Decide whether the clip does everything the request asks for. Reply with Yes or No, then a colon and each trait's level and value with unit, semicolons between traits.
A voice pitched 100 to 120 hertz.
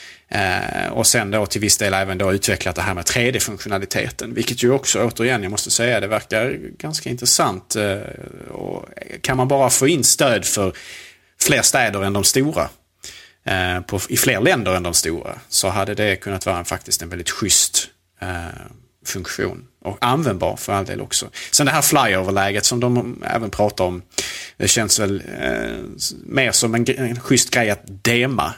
Yes: low, 105 Hz